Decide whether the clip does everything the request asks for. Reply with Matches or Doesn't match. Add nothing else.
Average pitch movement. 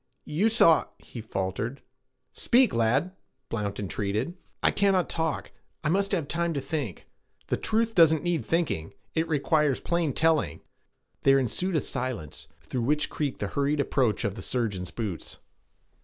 Doesn't match